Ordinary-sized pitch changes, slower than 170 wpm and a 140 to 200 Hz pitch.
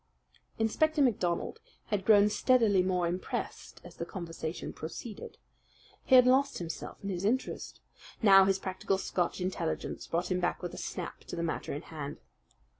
Yes: average, 4.1 semitones; average, 160 wpm; high, 190 Hz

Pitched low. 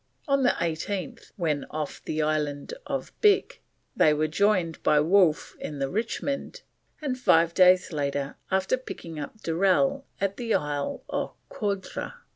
No: medium, 185 Hz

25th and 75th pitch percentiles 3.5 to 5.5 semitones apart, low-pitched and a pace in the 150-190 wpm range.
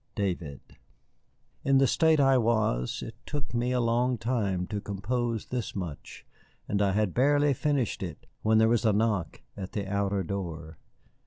Yes: average, 4.4 semitones; low, 110 Hz; average, 165 wpm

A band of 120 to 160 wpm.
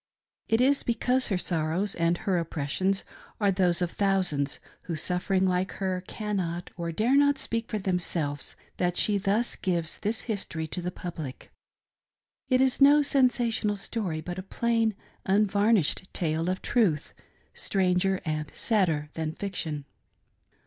Yes: average, 140 wpm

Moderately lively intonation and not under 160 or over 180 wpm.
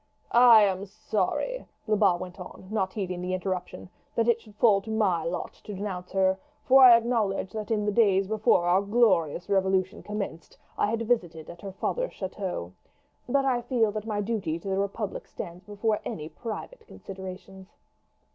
Yes: average, 3.0 semitones; average, 175 wpm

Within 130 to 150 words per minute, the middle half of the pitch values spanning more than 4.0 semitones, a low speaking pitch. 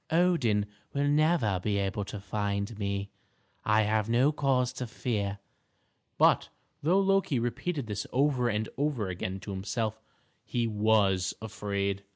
Yes: average, 140 wpm; average, 4.8 semitones; low, 110 Hz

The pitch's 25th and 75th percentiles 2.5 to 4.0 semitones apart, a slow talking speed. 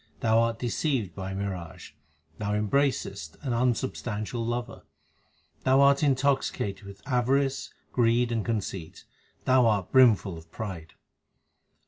No: average, 4.6 semitones; slow, 125 wpm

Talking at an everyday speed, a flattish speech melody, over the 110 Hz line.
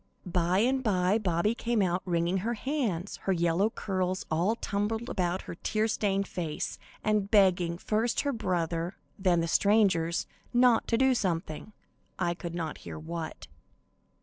No: average, 150 wpm; average, 4.1 semitones; high, 190 Hz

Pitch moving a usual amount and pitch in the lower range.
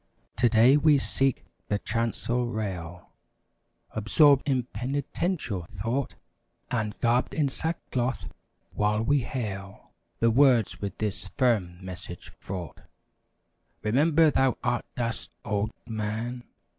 Yes: average, 4.2 semitones; low, 115 Hz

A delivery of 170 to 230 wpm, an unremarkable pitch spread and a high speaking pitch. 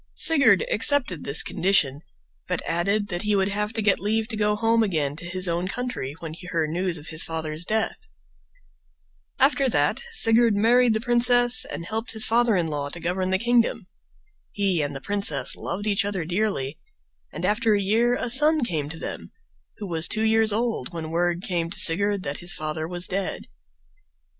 Yes: average, 190 wpm; average, 4.9 semitones; high, 200 Hz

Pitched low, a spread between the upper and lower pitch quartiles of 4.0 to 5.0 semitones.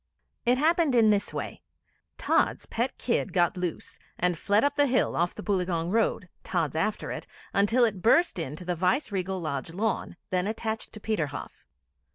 No: high, 200 Hz; average, 4.5 semitones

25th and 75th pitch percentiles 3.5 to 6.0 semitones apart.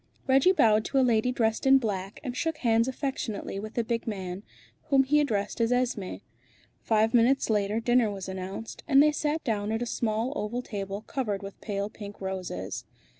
Yes: average, 3.9 semitones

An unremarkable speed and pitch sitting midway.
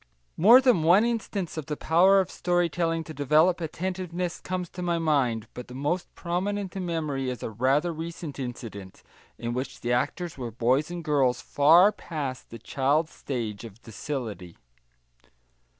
Yes: average, 165 wpm; medium, 155 Hz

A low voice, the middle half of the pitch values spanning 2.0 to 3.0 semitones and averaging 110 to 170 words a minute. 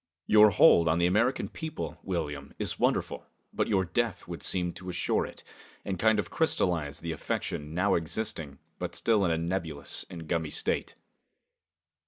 No: very low, 90 Hz; average, 3.9 semitones; average, 165 wpm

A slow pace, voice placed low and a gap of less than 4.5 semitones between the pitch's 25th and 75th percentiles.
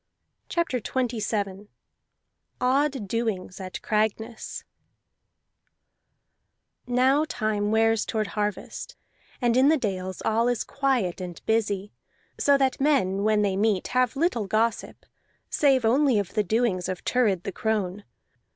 No: slow, 125 wpm; high, 220 Hz; average, 3.9 semitones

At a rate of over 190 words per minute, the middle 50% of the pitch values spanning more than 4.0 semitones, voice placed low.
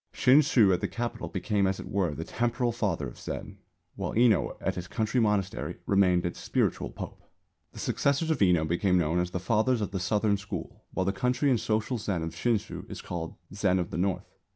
Yes: fast, 205 wpm; average, 4.5 semitones; low, 100 Hz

